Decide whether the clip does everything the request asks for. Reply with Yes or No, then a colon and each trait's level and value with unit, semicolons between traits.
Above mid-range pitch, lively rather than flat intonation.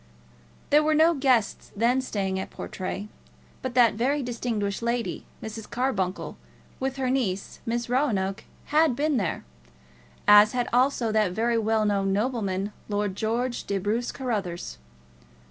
No: high, 230 Hz; average, 4.1 semitones